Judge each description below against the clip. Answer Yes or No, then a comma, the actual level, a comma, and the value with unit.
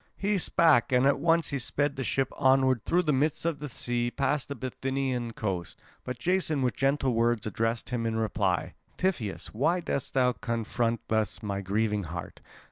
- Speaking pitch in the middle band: No, low, 125 Hz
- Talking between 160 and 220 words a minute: Yes, average, 180 wpm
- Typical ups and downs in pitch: Yes, average, 3.9 semitones